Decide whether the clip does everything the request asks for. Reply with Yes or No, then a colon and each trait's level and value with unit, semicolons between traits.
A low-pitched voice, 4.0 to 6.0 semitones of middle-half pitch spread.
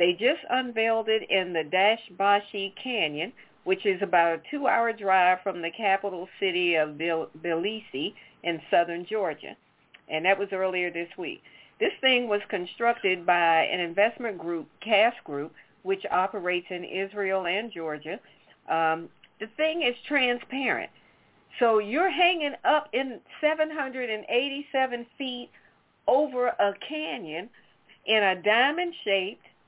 No: high, 200 Hz; wide, 5.5 semitones